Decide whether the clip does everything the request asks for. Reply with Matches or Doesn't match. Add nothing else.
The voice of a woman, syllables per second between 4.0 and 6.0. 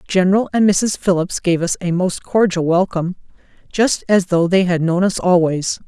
Matches